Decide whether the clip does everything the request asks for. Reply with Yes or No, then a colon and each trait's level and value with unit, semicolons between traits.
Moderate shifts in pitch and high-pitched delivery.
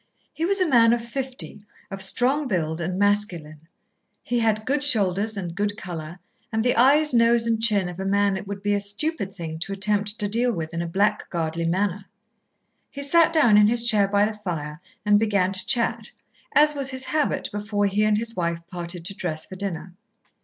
Yes: average, 4.3 semitones; high, 205 Hz